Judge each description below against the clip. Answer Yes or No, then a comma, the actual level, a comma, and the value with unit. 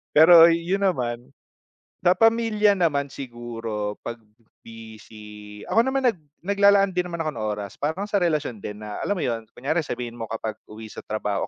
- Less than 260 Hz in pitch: Yes, medium, 140 Hz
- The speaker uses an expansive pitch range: Yes, wide, 8.8 semitones